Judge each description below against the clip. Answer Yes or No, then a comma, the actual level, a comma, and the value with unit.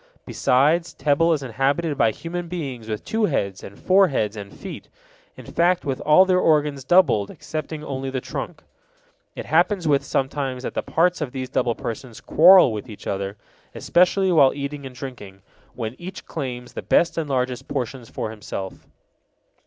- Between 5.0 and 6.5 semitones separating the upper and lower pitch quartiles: Yes, wide, 5.4 semitones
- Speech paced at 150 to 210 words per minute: Yes, average, 170 wpm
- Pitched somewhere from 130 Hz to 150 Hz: Yes, medium, 140 Hz